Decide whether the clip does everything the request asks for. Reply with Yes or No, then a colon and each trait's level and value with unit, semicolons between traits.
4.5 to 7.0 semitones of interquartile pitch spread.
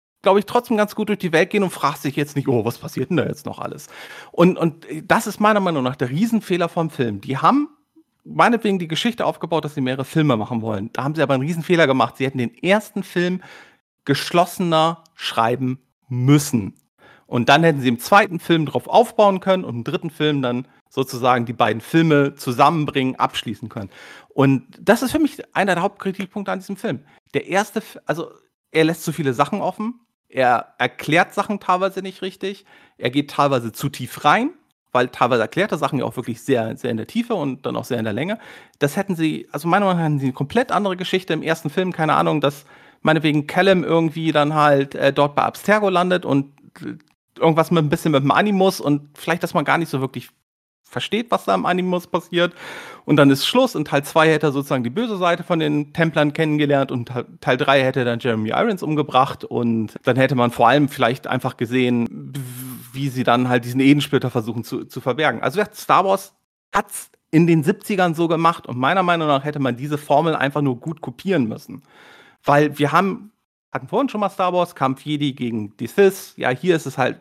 Yes: wide, 5.4 semitones